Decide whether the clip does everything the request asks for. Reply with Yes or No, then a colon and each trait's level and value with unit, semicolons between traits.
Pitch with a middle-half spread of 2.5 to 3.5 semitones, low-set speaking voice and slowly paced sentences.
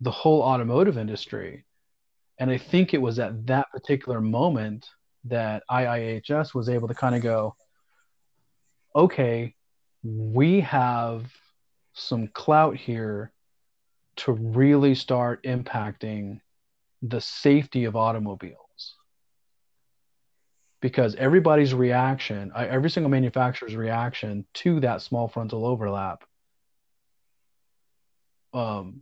Yes: average, 3.1 semitones; low, 125 Hz; slow, 100 wpm